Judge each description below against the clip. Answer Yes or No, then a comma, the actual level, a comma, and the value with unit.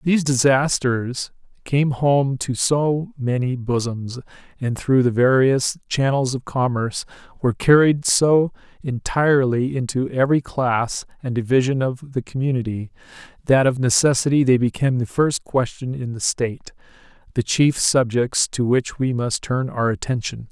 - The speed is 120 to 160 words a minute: Yes, average, 140 wpm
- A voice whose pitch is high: No, low, 130 Hz